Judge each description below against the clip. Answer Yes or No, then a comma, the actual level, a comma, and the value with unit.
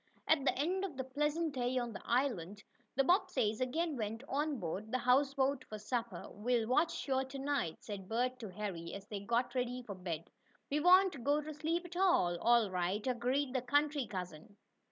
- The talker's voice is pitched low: No, very high, 250 Hz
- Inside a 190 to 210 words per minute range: Yes, average, 195 wpm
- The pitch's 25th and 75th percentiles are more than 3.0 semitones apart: Yes, wide, 5.4 semitones